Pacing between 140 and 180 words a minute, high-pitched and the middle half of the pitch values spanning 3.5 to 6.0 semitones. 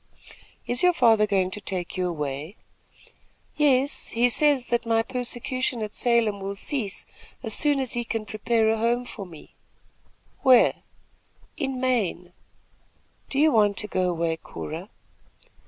Yes: average, 145 wpm; high, 225 Hz; average, 4.5 semitones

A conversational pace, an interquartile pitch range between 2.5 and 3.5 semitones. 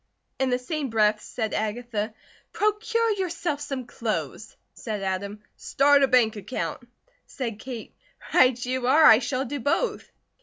No: average, 145 wpm; average, 4.6 semitones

